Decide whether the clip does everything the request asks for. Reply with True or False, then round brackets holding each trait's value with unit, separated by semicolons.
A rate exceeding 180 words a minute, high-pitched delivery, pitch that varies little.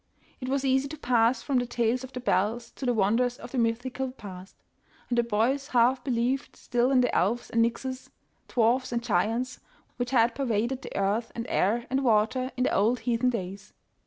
True (200 wpm; 240 Hz; 2.1 semitones)